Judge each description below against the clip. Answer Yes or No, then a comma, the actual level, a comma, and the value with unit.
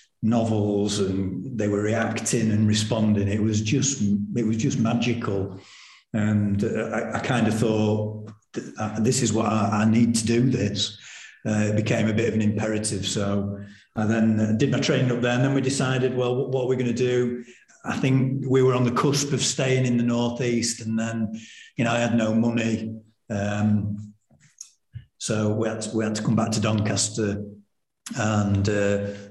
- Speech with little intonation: Yes, narrow, 2.2 semitones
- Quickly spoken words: No, average, 185 wpm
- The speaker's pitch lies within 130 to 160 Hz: No, low, 110 Hz